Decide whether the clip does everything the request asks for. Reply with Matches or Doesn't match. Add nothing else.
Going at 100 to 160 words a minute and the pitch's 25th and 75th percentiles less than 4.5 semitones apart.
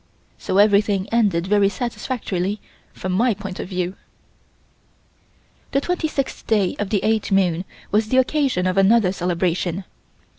Matches